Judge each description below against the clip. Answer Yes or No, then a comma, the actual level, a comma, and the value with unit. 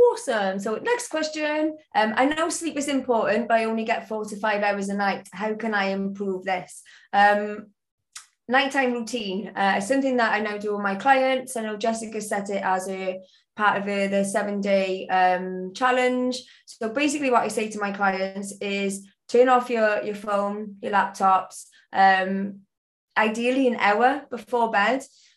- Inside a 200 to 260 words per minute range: No, average, 175 wpm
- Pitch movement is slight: No, average, 3.9 semitones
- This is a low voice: No, high, 210 Hz